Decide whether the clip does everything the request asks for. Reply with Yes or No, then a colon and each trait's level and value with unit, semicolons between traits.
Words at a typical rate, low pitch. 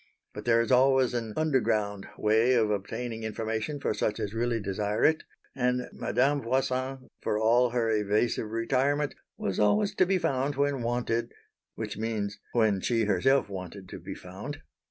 Yes: average, 160 wpm; low, 115 Hz